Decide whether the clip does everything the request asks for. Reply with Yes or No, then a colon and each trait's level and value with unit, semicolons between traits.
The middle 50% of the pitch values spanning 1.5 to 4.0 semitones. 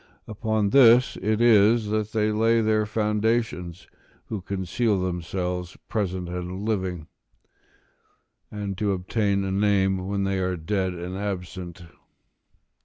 Yes: average, 2.8 semitones